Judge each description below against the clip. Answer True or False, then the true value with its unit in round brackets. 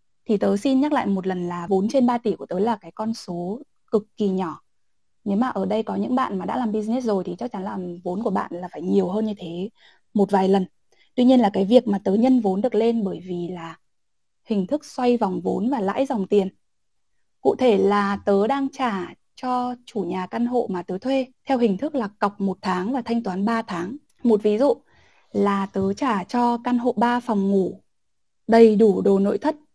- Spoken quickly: False (230 wpm)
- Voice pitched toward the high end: True (205 Hz)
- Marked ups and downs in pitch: False (4.2 semitones)